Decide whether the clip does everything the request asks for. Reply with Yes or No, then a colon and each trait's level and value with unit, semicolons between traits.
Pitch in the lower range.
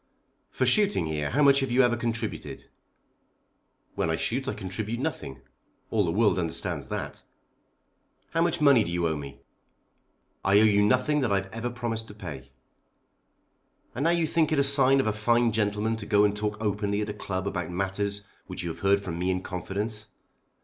Yes: low, 105 Hz